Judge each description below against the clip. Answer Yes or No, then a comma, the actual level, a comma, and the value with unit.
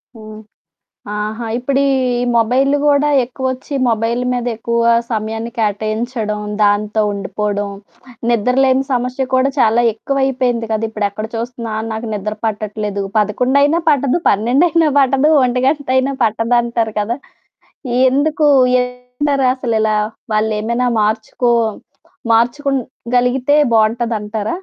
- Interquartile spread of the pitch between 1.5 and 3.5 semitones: Yes, average, 3.2 semitones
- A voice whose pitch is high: Yes, high, 235 Hz